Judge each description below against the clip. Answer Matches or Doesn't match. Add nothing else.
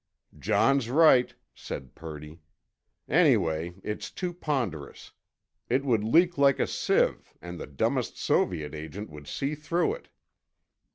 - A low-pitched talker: Matches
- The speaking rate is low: Matches